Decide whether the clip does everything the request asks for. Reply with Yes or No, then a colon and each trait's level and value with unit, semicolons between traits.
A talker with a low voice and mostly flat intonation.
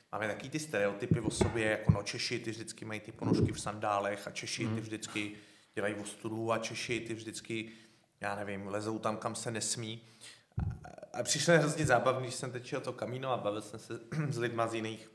Yes: low, 115 Hz; narrow, 2.2 semitones